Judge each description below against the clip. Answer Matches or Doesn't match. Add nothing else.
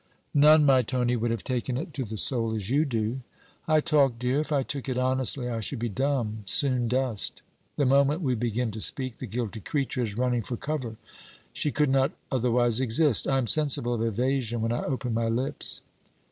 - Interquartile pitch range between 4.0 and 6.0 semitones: Doesn't match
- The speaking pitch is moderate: Doesn't match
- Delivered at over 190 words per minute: Matches